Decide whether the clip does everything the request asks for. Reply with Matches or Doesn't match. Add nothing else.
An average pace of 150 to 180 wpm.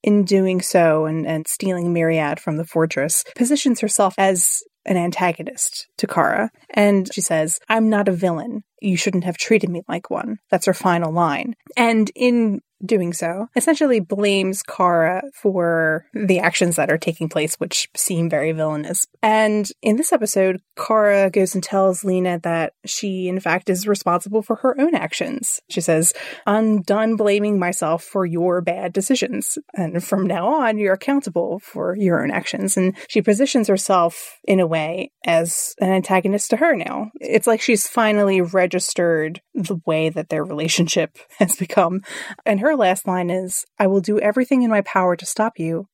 Matches